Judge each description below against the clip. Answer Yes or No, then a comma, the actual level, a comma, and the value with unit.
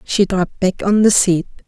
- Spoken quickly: Yes, fast, 215 wpm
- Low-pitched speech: No, high, 190 Hz